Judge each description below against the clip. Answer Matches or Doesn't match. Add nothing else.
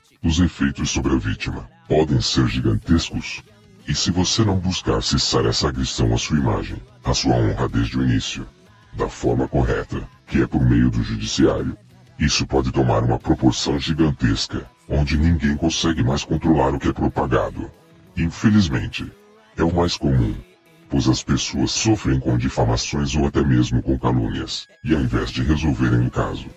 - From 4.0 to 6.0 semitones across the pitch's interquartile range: Matches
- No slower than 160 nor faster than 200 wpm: Matches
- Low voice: Matches